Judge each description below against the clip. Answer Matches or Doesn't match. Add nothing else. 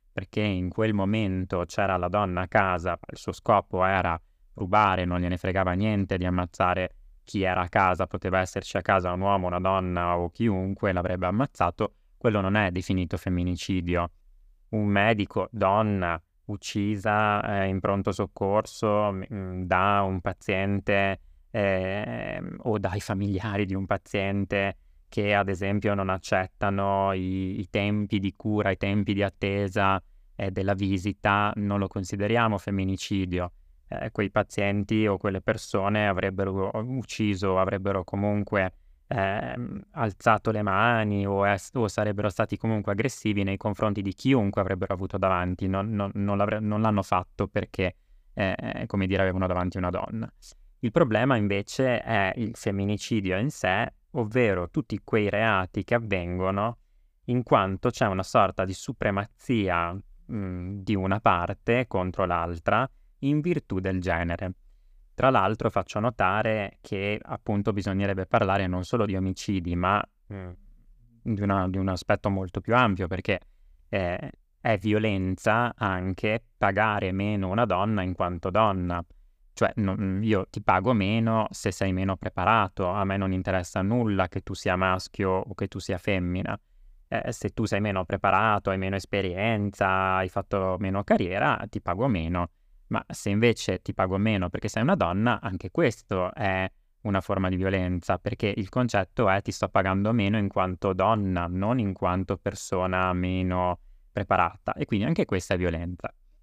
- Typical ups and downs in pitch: Doesn't match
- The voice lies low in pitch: Matches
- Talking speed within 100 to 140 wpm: Doesn't match